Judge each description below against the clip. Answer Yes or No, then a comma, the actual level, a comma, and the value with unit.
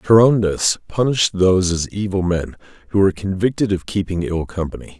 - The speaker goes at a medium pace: Yes, average, 155 wpm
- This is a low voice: Yes, very low, 95 Hz